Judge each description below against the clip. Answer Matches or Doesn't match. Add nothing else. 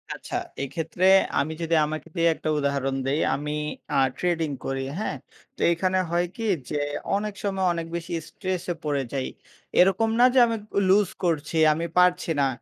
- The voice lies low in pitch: Doesn't match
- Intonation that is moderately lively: Matches